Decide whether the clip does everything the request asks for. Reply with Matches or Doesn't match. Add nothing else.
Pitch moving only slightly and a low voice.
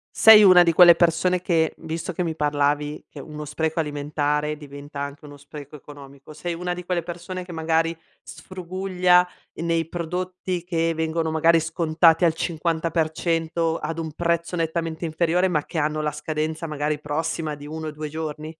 Doesn't match